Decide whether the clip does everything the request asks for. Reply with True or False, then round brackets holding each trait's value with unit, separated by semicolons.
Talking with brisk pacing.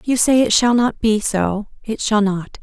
True (250 wpm)